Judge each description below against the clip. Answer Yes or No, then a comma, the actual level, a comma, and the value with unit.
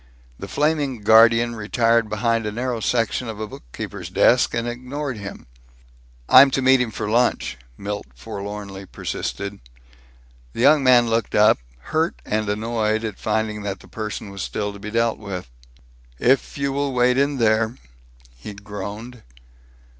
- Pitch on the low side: Yes, low, 115 Hz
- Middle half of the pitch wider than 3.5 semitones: No, average, 3.1 semitones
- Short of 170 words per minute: Yes, average, 155 wpm